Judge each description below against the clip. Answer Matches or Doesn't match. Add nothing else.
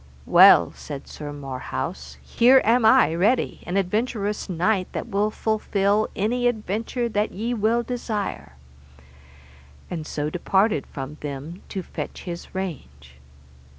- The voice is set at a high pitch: Matches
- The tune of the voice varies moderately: Doesn't match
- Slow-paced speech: Matches